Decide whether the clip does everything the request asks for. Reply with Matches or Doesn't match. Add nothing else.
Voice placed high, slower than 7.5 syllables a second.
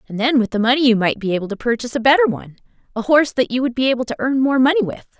Doesn't match